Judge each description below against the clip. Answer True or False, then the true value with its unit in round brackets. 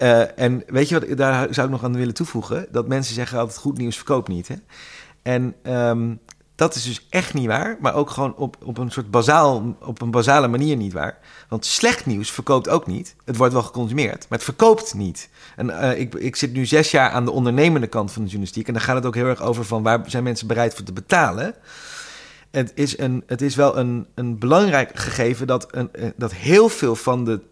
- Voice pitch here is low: True (125 Hz)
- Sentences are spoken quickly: True (230 wpm)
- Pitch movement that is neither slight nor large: True (3.2 semitones)